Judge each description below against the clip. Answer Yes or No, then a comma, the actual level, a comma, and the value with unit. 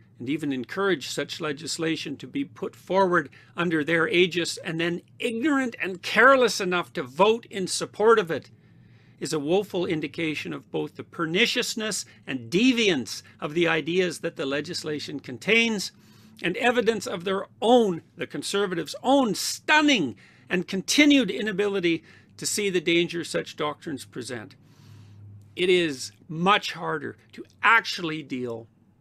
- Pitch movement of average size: No, wide, 6.2 semitones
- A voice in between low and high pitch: Yes, medium, 170 Hz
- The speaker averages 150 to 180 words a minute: No, average, 140 wpm